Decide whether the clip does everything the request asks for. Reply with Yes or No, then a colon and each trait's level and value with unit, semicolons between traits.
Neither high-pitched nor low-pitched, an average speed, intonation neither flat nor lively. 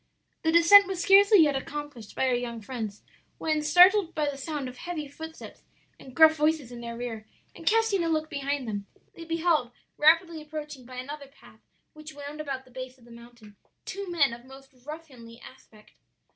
No: very high, 290 Hz; average, 185 wpm; average, 4.4 semitones